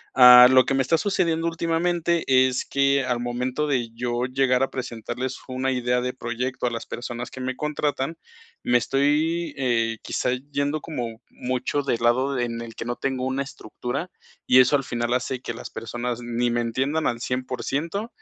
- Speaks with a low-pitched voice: Yes, low, 130 Hz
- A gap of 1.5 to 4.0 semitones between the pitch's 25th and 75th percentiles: Yes, narrow, 2.6 semitones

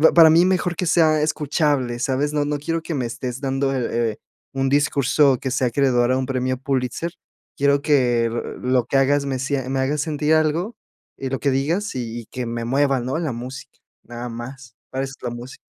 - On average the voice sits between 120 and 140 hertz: Yes, low, 135 Hz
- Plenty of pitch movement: No, average, 2.9 semitones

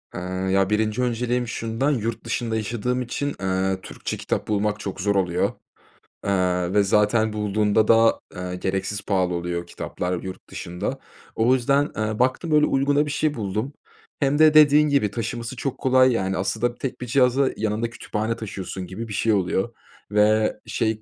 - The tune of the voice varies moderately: Yes, average, 4.4 semitones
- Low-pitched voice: Yes, low, 110 Hz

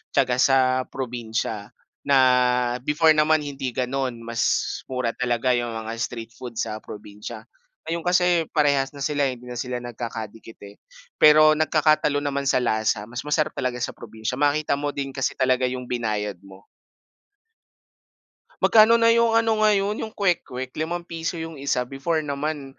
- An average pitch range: Yes, average, 4.3 semitones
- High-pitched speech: No, low, 135 Hz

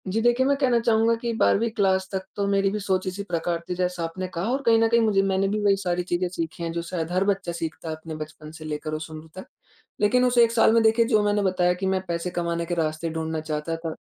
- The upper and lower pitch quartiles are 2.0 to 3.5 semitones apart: No, average, 4.1 semitones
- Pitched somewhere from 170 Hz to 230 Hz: Yes, medium, 185 Hz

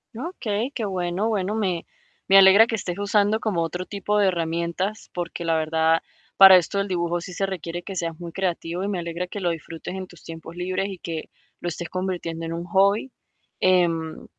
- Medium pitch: Yes, medium, 180 Hz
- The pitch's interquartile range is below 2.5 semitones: No, average, 2.8 semitones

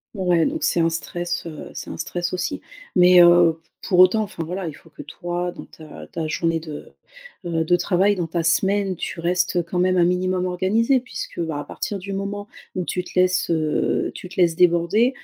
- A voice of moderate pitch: Yes, medium, 180 Hz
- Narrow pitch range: Yes, narrow, 2.0 semitones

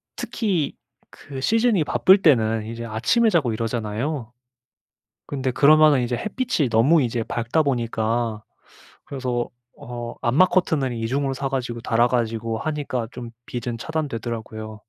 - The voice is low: Yes, low, 125 Hz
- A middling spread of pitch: Yes, average, 4.4 semitones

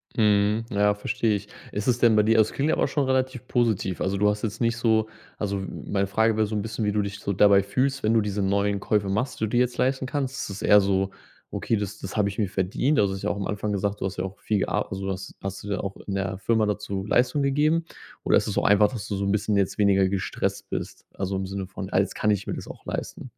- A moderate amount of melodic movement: No, narrow, 2.3 semitones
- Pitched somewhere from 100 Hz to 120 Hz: Yes, low, 105 Hz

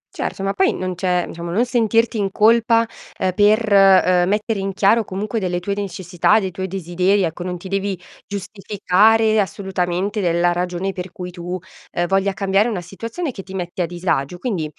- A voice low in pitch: No, high, 190 Hz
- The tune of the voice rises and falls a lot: No, average, 2.7 semitones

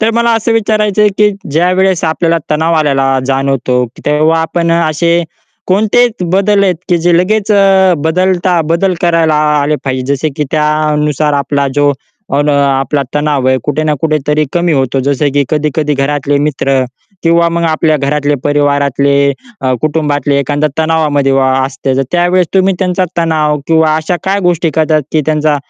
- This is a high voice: No, medium, 155 Hz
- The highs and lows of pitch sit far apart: No, average, 3.3 semitones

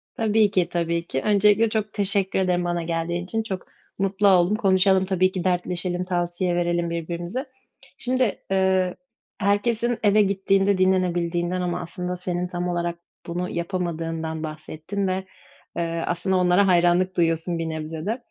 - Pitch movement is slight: Yes, narrow, 2.2 semitones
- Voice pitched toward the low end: No, medium, 180 Hz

